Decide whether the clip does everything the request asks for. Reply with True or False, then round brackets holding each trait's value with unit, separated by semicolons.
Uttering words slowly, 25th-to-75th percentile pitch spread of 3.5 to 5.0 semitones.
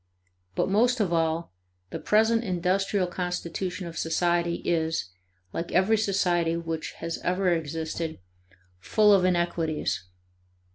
False (115 wpm; 2.8 semitones)